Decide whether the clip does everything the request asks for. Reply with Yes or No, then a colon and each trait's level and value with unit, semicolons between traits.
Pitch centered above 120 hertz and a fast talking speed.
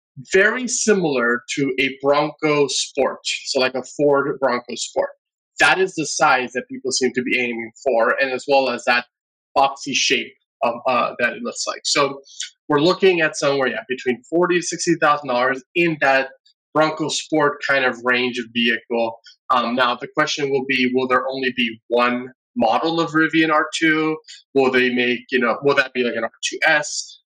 No: low, 135 Hz; average, 180 wpm